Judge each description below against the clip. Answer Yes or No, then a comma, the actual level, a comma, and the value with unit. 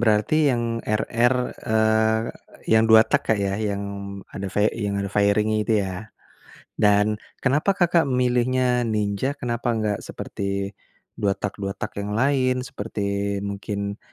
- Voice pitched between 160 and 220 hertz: No, low, 110 Hz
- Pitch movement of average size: Yes, average, 3.3 semitones